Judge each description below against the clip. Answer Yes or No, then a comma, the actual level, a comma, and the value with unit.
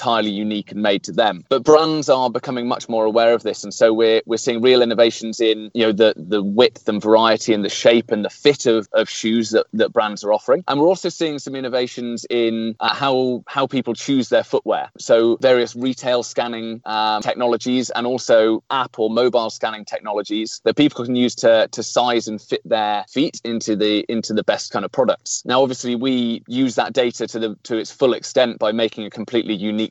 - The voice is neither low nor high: No, low, 115 Hz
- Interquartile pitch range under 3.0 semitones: Yes, narrow, 2.4 semitones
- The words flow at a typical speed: No, fast, 215 wpm